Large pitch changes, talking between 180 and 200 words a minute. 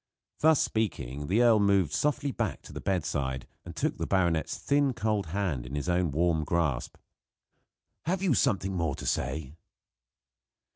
No: wide, 6.5 semitones; average, 155 wpm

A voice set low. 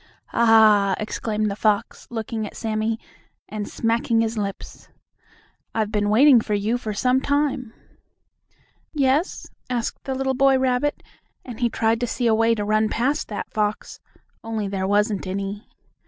No: high, 225 Hz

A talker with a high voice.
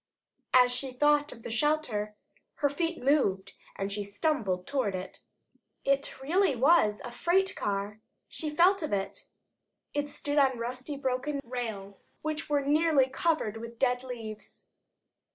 Yes: very high, 260 Hz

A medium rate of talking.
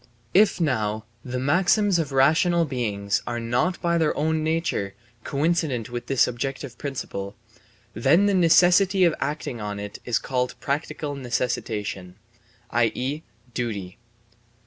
No: slow, 125 wpm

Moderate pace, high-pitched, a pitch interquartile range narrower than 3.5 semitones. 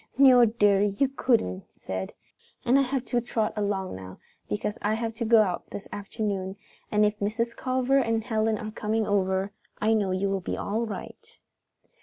Yes: average, 190 wpm; high, 215 Hz; average, 2.8 semitones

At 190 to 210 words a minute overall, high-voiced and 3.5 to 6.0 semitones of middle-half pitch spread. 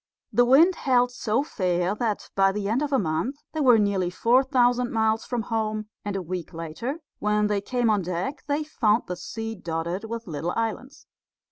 Yes: average, 195 wpm; high, 220 Hz; average, 4.6 semitones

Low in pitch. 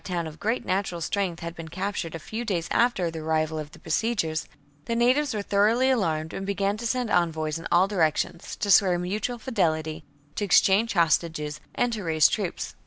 No: medium, 180 Hz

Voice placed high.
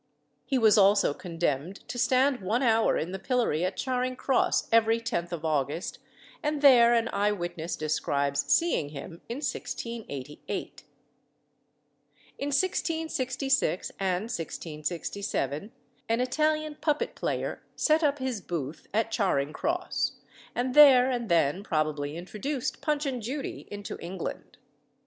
Yes: high, 220 Hz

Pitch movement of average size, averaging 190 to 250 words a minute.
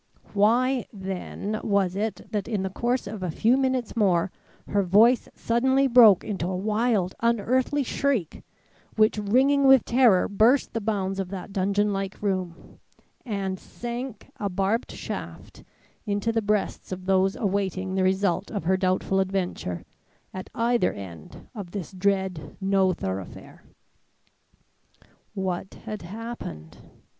No: average, 3.5 semitones; slow, 135 wpm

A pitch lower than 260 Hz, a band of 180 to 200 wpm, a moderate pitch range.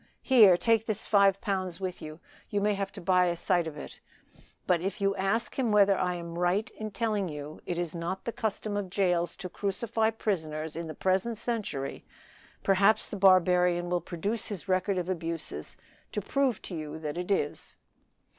Yes: medium, 185 Hz; average, 190 wpm; average, 3.1 semitones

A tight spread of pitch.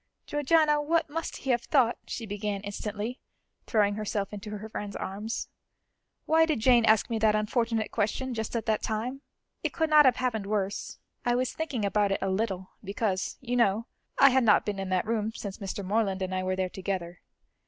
No: average, 3.7 semitones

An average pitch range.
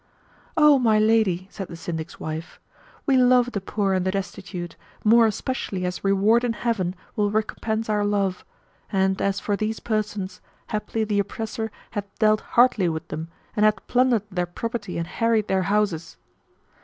Yes: average, 3.0 semitones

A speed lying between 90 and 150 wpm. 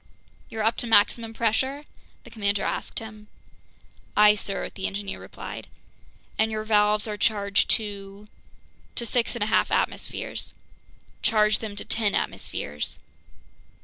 Yes: average, 140 wpm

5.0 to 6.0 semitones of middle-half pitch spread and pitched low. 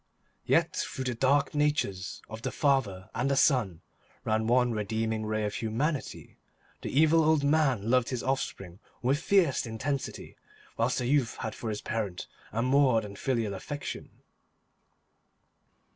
No: average, 4.2 semitones; low, 125 Hz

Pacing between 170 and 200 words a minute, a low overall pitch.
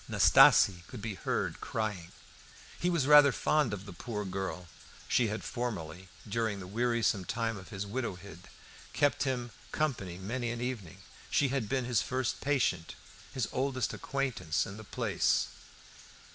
No: average, 150 wpm; low, 115 Hz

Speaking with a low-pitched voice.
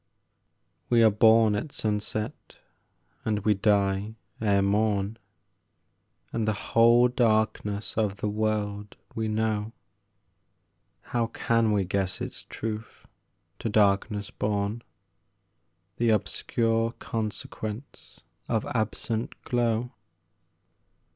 Yes: low, 110 Hz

